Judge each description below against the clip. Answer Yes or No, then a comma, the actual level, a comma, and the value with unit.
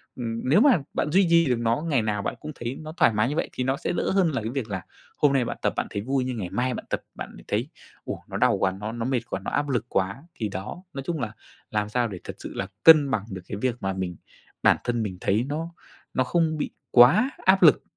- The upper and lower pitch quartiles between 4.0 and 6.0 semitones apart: Yes, wide, 5.6 semitones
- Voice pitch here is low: Yes, low, 125 Hz